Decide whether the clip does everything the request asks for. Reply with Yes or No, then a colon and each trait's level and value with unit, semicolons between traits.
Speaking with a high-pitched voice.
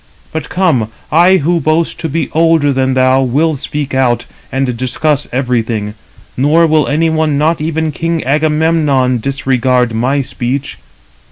No: medium, 145 Hz